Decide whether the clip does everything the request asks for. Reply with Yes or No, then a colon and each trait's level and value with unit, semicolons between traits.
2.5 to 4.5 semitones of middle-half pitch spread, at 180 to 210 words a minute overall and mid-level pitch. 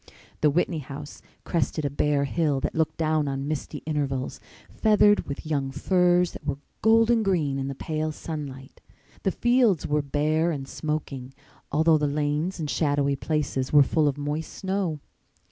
No: average, 2.8 semitones; average, 160 wpm; medium, 150 Hz